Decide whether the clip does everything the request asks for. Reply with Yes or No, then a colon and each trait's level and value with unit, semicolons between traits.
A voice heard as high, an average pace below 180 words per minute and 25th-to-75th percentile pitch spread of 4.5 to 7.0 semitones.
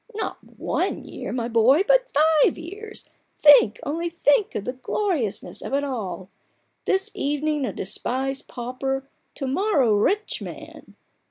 Yes: very high, 280 Hz; average, 150 wpm; wide, 5.4 semitones